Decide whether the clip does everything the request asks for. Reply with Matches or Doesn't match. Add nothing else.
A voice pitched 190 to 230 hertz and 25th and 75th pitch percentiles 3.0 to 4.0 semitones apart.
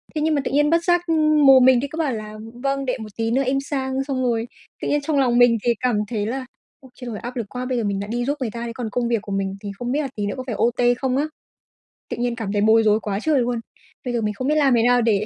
Doesn't match